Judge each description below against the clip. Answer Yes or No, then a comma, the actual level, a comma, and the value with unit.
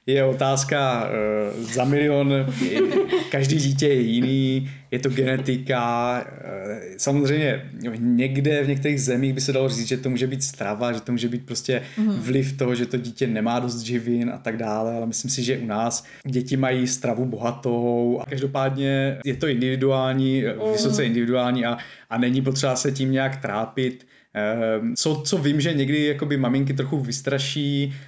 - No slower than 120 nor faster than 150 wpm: No, average, 160 wpm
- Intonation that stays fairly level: Yes, narrow, 2.3 semitones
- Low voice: Yes, low, 130 Hz